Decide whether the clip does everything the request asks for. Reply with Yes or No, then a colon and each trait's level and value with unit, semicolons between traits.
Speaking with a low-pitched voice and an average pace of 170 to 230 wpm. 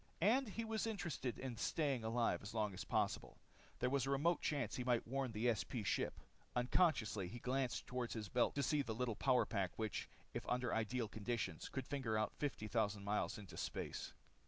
Yes: low, 120 Hz; average, 195 wpm